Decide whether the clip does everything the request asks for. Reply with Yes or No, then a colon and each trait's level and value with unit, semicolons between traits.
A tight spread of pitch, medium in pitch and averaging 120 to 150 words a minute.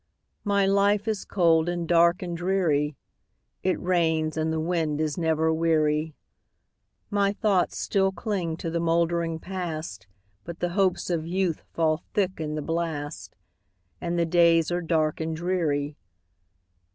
Yes: narrow, 2.2 semitones; medium, 170 Hz; average, 145 wpm